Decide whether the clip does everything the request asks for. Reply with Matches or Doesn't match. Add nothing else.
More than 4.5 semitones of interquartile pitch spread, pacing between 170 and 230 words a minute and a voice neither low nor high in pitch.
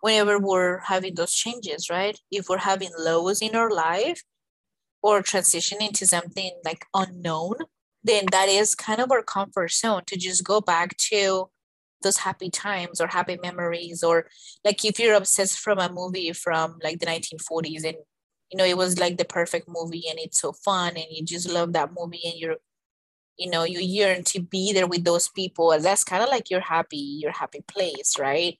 Doesn't match